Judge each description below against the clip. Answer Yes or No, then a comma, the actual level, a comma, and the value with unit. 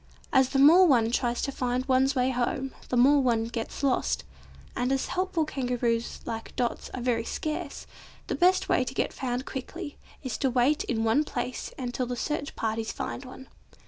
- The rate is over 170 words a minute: Yes, average, 185 wpm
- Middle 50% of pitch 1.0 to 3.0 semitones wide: Yes, narrow, 2.5 semitones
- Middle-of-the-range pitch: No, very high, 255 Hz